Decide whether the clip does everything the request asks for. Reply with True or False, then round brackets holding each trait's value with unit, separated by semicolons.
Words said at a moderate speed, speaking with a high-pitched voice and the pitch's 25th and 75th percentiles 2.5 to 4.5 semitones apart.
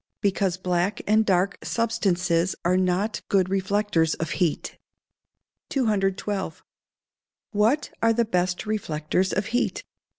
False (120 wpm; 195 Hz; 2.9 semitones)